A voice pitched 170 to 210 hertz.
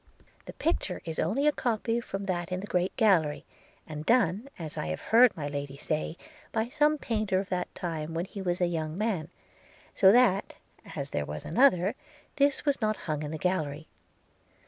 Yes: medium, 185 Hz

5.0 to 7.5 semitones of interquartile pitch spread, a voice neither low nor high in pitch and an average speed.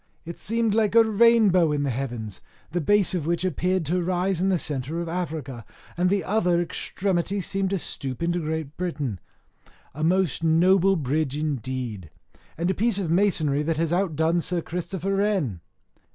No: average, 4.1 semitones; medium, 170 Hz; average, 170 wpm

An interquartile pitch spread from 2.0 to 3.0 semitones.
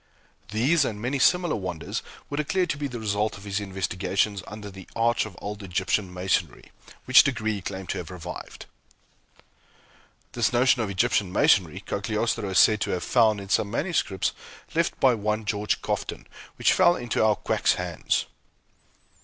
No: average, 3.7 semitones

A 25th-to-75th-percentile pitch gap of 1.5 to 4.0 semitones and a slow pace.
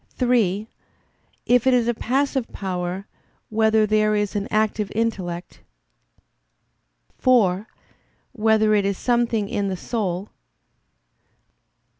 Yes: average, 2.8 semitones; slow, 105 wpm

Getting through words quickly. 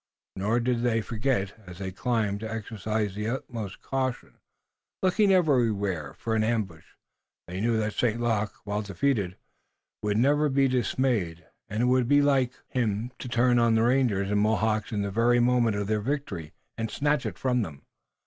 No: average, 175 wpm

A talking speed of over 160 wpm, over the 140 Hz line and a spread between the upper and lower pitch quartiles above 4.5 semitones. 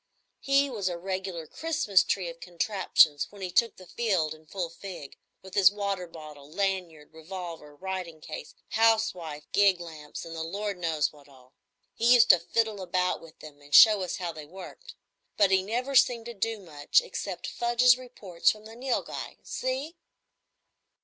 Yes: average, 175 wpm; medium, 185 Hz; average, 5.2 semitones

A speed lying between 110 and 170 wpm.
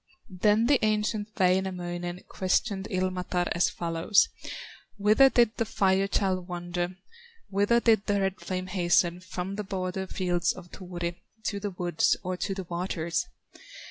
Yes: average, 140 wpm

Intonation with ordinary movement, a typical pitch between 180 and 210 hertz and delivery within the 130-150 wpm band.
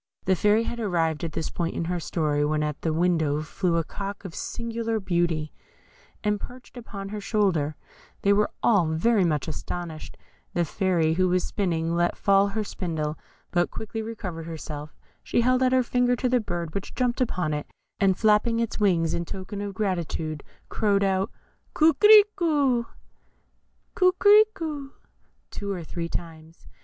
No: average, 5.0 semitones; medium, 185 Hz; average, 160 wpm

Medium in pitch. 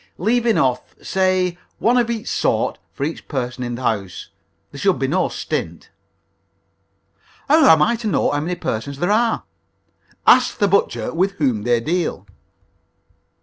Yes: medium, 170 Hz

